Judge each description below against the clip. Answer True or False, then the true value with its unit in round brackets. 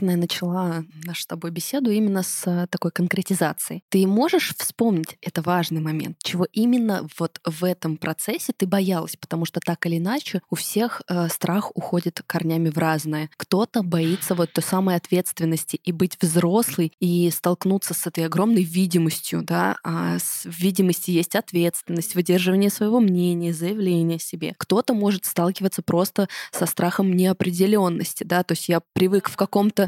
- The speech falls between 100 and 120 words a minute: False (155 wpm)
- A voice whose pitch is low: False (180 Hz)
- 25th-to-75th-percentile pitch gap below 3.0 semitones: True (2.4 semitones)